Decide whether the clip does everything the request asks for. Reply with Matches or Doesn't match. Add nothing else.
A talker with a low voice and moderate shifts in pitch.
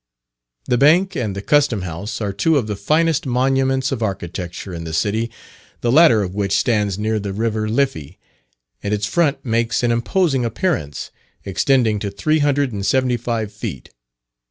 Matches